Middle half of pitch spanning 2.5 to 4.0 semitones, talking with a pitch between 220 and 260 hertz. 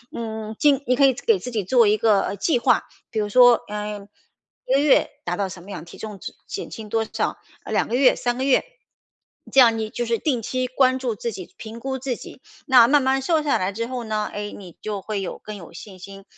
Yes: average, 3.7 semitones; high, 230 Hz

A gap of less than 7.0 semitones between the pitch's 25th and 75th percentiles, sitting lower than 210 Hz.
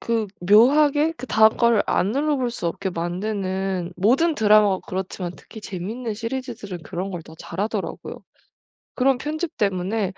No: average, 5.1 semitones; high, 215 Hz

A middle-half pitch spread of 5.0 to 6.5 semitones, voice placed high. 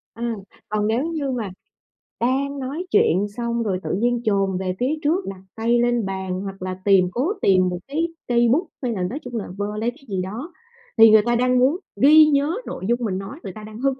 Yes: average, 5.3 semitones; high, 235 Hz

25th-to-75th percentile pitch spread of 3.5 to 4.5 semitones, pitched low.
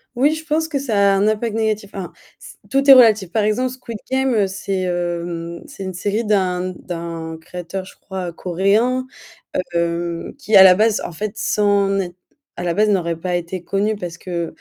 No: average, 3.8 semitones; high, 195 Hz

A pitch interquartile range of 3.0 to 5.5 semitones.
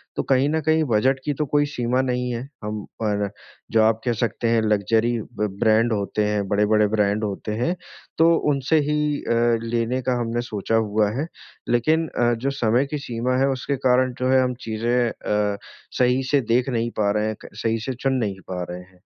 Yes: average, 3.3 semitones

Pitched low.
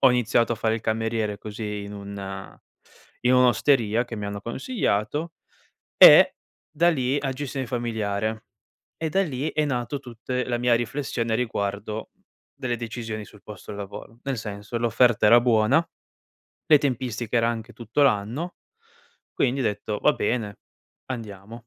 Yes: low, 115 Hz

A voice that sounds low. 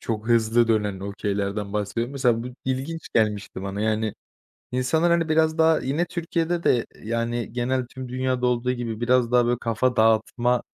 Yes: low, 120 Hz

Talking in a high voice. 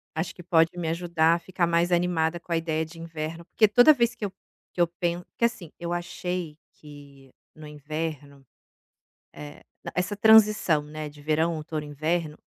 No: medium, 165 Hz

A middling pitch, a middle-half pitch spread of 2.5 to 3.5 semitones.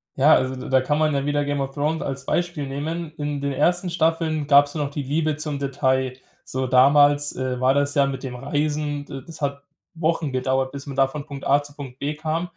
No: medium, 145 Hz; narrow, 2.0 semitones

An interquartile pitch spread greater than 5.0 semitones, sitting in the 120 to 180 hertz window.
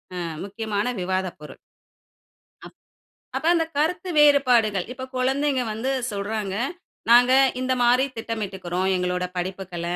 No: wide, 5.5 semitones; high, 220 Hz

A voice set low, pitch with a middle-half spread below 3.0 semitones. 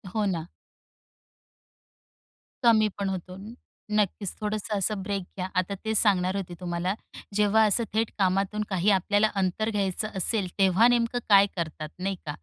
No: high, 200 Hz; narrow, 2.6 semitones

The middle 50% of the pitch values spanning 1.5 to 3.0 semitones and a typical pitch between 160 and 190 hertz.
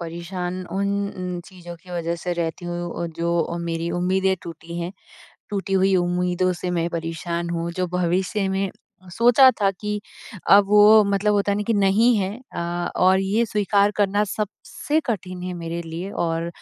Yes: average, 2.7 semitones; medium, 185 Hz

